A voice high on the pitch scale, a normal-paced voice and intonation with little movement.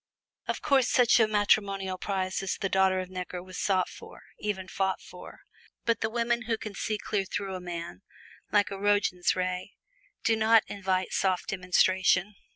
Yes: high, 195 Hz; average, 170 wpm; narrow, 2.3 semitones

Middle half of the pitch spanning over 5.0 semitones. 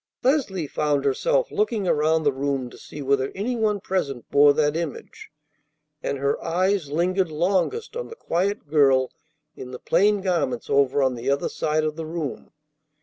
Yes: wide, 5.5 semitones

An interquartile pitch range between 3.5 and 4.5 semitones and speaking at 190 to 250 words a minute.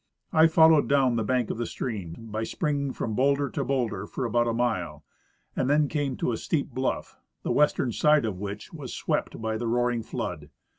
Yes: average, 4.0 semitones; average, 200 wpm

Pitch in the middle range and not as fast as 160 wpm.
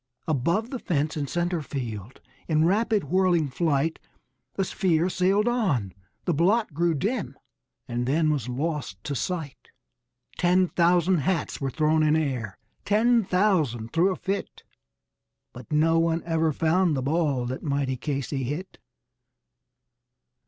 Yes: medium, 160 Hz; average, 140 wpm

